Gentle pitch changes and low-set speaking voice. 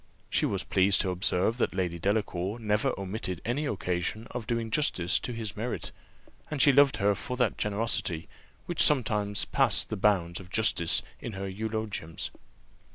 No: average, 3.8 semitones; low, 105 Hz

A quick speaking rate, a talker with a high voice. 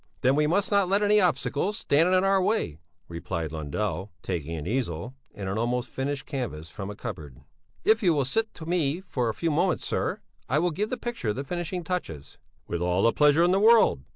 No: fast, 210 wpm; medium, 140 Hz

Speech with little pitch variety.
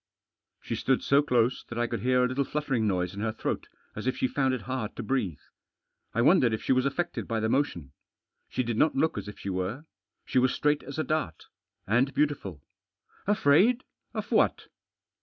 No: average, 4.3 semitones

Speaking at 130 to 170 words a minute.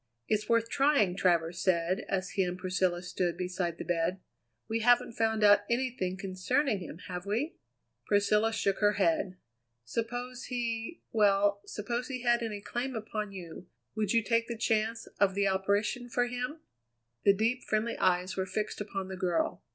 Yes: average, 165 wpm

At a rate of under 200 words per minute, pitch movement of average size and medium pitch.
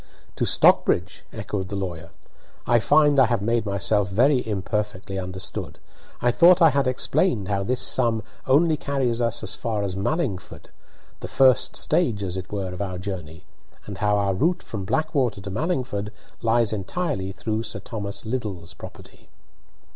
No: average, 160 wpm; average, 4.9 semitones; low, 110 Hz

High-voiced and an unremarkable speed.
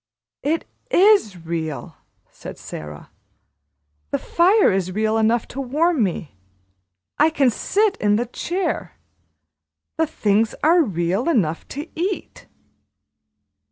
No: high, 240 Hz; slow, 115 wpm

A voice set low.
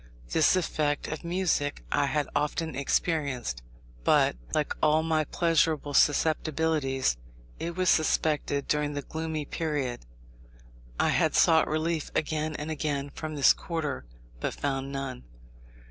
No: medium, 150 Hz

